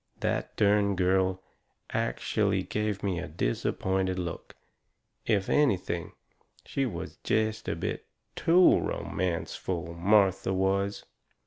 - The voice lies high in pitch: No, very low, 95 Hz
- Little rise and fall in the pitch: Yes, narrow, 2.1 semitones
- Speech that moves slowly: Yes, slow, 105 wpm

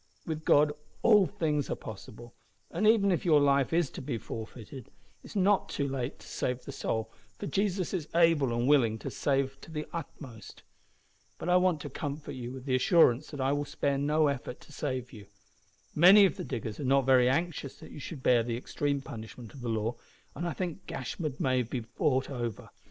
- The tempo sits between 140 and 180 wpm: No, fast, 205 wpm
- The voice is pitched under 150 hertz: Yes, medium, 140 Hz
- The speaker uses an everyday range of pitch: Yes, average, 4.6 semitones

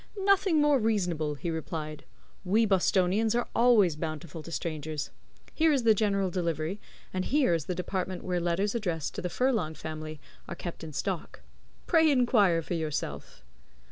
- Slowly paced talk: No, average, 160 wpm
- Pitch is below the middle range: No, medium, 180 Hz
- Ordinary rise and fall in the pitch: No, wide, 5.7 semitones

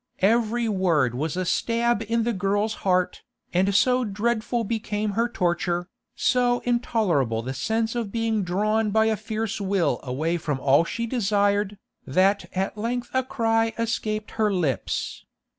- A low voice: No, high, 210 Hz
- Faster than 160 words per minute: No, average, 150 wpm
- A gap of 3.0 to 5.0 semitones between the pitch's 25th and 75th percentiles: Yes, average, 3.9 semitones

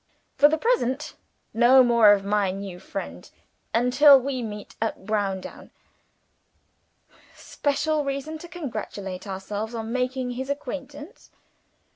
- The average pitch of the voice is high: Yes, high, 245 Hz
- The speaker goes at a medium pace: No, slow, 115 wpm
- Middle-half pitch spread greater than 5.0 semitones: Yes, wide, 5.4 semitones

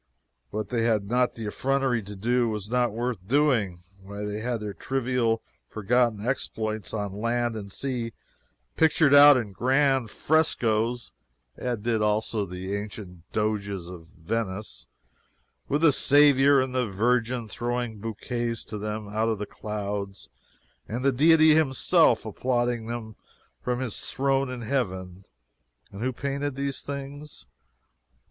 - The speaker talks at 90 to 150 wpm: Yes, average, 140 wpm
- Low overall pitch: Yes, low, 115 Hz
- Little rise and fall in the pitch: No, average, 3.9 semitones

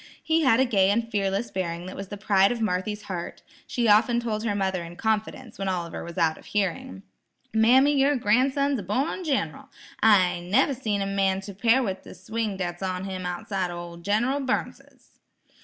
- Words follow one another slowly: No, average, 195 wpm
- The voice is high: Yes, high, 205 Hz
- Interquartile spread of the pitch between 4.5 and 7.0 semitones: No, average, 4.0 semitones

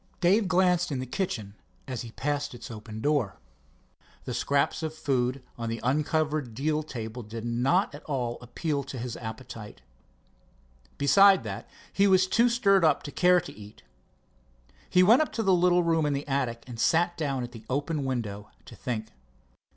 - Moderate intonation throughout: No, wide, 6.5 semitones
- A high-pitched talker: No, medium, 140 Hz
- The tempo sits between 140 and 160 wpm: No, average, 175 wpm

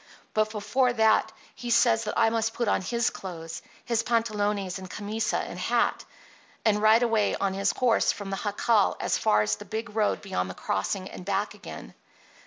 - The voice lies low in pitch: No, high, 210 Hz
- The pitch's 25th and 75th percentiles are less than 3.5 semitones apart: Yes, narrow, 2.5 semitones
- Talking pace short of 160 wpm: No, average, 190 wpm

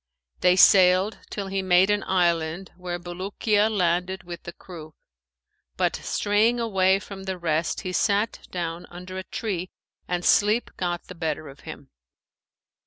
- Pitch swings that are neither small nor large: No, narrow, 2.2 semitones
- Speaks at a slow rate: No, average, 150 wpm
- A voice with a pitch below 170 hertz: No, medium, 185 Hz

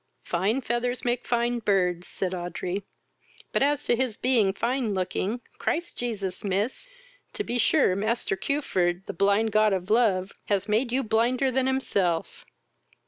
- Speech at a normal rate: Yes, average, 150 wpm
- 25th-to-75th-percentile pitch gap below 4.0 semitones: No, average, 4.3 semitones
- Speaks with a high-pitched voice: Yes, high, 220 Hz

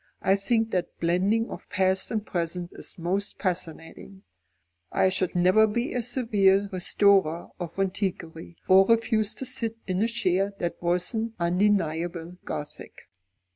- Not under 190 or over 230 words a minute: No, slow, 135 wpm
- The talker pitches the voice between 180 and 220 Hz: Yes, high, 190 Hz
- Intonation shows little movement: No, average, 3.7 semitones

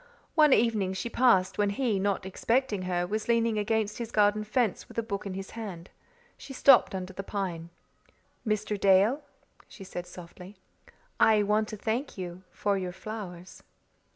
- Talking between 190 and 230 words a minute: No, average, 165 wpm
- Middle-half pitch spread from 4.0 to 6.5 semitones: No, average, 3.0 semitones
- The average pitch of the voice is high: Yes, high, 205 Hz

